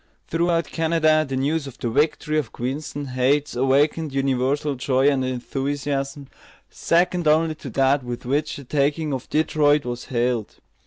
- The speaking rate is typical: Yes, average, 150 wpm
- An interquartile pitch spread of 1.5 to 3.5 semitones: Yes, average, 2.7 semitones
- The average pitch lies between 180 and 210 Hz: No, medium, 140 Hz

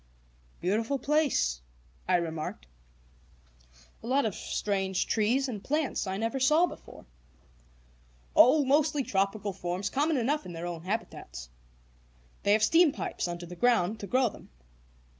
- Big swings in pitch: Yes, wide, 7.4 semitones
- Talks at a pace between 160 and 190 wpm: No, average, 140 wpm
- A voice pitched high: Yes, high, 210 Hz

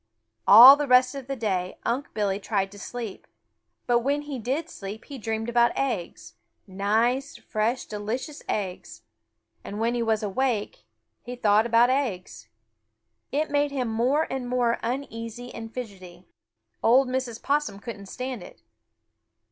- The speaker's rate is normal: Yes, average, 150 wpm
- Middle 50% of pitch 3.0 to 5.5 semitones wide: Yes, average, 3.8 semitones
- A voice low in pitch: No, high, 235 Hz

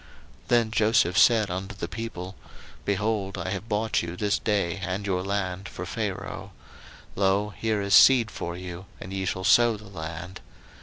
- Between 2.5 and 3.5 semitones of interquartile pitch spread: Yes, average, 2.8 semitones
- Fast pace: No, average, 170 wpm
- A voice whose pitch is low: Yes, low, 100 Hz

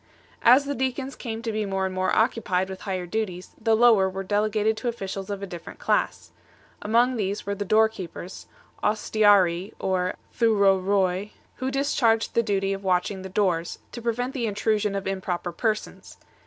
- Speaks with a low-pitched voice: No, high, 205 Hz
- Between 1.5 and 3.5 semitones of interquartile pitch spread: Yes, average, 2.9 semitones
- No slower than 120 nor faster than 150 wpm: No, average, 170 wpm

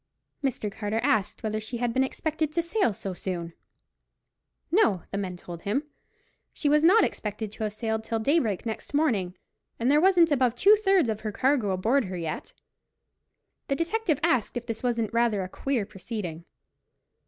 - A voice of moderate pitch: No, high, 230 Hz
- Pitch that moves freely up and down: Yes, wide, 6.1 semitones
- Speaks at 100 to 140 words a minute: No, average, 175 wpm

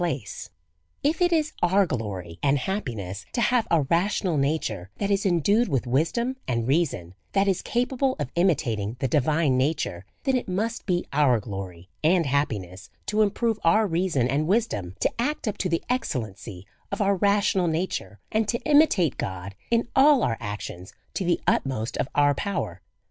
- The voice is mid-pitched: Yes, medium, 165 Hz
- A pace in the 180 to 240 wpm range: Yes, average, 185 wpm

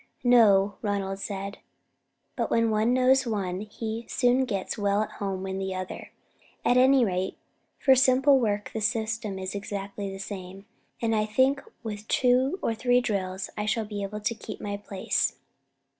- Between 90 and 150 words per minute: No, average, 170 wpm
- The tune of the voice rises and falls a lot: No, average, 3.7 semitones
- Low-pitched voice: No, high, 210 Hz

